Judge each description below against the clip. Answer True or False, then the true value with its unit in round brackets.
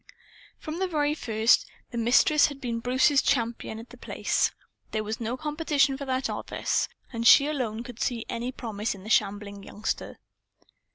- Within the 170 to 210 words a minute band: True (175 wpm)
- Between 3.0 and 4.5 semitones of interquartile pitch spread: True (4.1 semitones)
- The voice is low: False (240 Hz)